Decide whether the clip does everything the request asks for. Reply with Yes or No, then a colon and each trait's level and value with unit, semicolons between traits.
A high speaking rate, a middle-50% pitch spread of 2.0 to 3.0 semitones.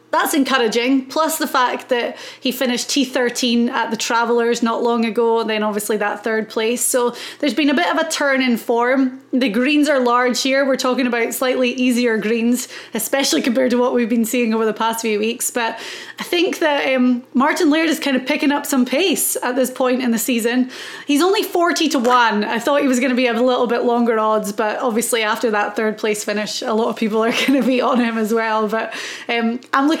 Yes: fast, 230 wpm; average, 2.7 semitones